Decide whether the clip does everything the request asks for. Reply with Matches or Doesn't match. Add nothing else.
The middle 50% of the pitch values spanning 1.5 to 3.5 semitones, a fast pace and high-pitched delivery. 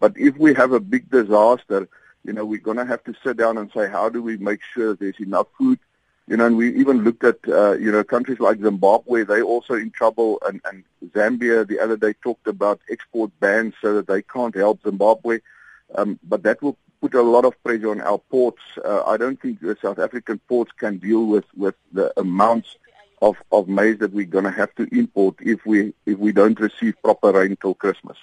Doesn't match